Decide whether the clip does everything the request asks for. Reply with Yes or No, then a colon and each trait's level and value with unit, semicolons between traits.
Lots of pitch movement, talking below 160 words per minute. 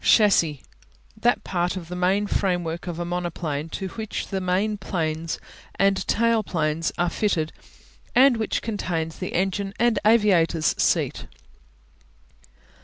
No: average, 3.9 semitones; average, 140 wpm